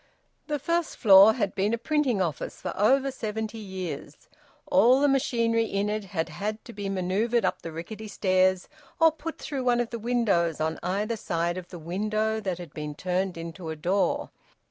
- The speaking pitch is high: Yes, high, 205 Hz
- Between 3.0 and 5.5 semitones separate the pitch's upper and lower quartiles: Yes, average, 4.4 semitones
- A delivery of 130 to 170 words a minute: No, average, 190 wpm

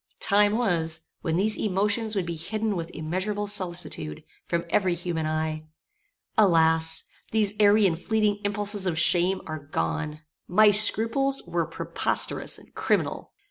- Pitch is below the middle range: No, medium, 185 Hz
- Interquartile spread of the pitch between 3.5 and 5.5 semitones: Yes, average, 4.3 semitones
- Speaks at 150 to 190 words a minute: No, average, 140 wpm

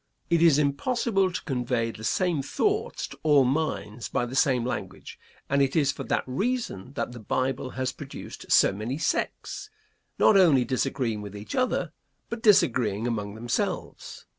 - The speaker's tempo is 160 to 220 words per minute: Yes, average, 165 wpm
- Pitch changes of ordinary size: No, wide, 6.1 semitones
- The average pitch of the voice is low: Yes, low, 130 Hz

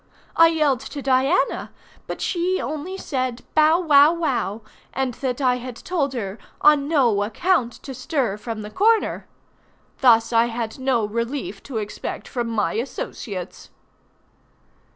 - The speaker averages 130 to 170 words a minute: Yes, average, 140 wpm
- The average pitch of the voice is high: Yes, very high, 260 Hz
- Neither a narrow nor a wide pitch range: Yes, average, 4.8 semitones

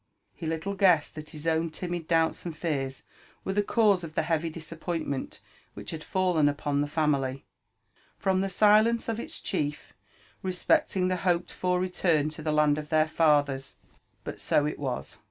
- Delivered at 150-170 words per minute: No, average, 180 wpm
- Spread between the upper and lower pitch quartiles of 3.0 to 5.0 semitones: Yes, average, 3.4 semitones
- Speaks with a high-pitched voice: No, medium, 160 Hz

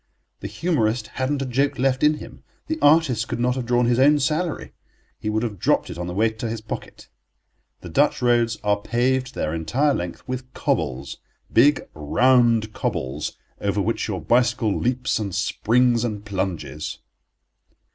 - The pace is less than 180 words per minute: Yes, average, 165 wpm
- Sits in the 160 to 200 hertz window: No, low, 120 Hz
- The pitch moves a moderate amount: Yes, average, 3.8 semitones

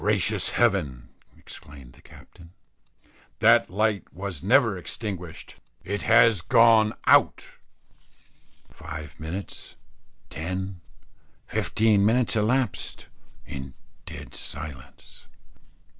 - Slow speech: Yes, slow, 85 wpm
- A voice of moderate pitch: No, very low, 95 Hz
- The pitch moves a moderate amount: No, wide, 6.0 semitones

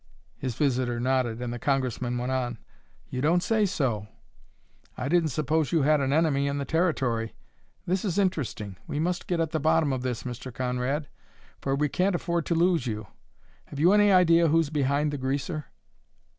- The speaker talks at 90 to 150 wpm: No, average, 185 wpm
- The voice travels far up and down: No, average, 4.5 semitones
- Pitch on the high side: No, medium, 140 Hz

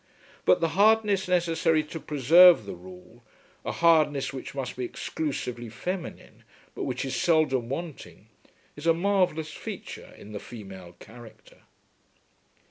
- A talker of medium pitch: Yes, medium, 150 Hz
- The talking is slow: Yes, slow, 130 wpm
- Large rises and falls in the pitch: Yes, wide, 5.9 semitones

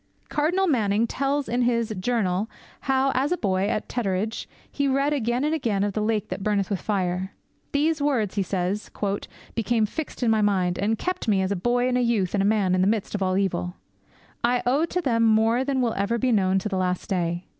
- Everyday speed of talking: No, fast, 210 wpm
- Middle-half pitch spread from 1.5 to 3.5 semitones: No, average, 4.5 semitones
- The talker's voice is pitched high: Yes, high, 220 Hz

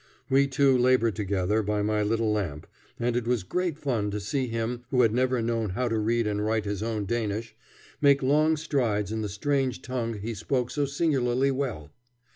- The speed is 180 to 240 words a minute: Yes, average, 195 wpm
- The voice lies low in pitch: Yes, low, 115 Hz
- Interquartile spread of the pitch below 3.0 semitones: No, average, 3.7 semitones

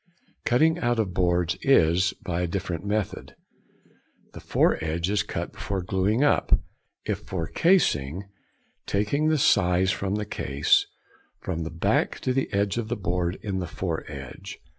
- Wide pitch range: No, average, 3.9 semitones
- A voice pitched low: Yes, very low, 95 Hz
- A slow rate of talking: No, average, 150 wpm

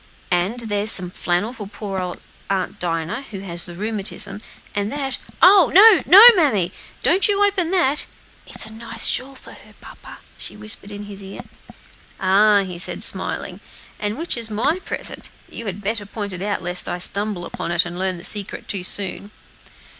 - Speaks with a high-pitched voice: Yes, high, 205 Hz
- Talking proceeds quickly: No, average, 185 wpm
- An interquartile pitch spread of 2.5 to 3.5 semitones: No, average, 3.9 semitones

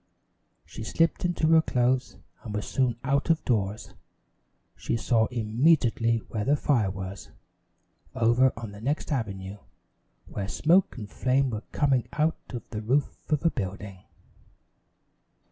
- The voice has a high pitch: No, low, 120 Hz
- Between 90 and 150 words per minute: Yes, average, 140 wpm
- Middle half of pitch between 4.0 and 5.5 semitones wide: Yes, average, 4.8 semitones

